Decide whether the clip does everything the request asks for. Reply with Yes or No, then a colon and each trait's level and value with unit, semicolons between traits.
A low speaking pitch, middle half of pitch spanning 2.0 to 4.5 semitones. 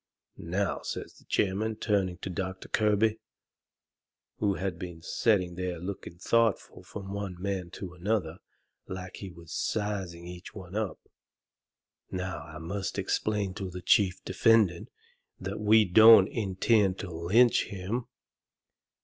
Yes: very low, 95 Hz; average, 2.7 semitones